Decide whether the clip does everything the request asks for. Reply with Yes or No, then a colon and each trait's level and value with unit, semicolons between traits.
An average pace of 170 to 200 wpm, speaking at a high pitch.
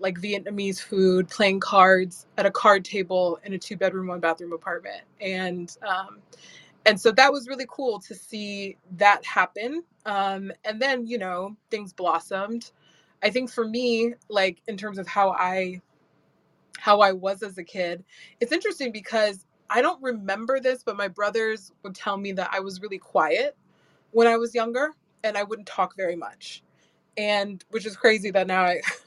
Yes: average, 175 wpm; high, 200 Hz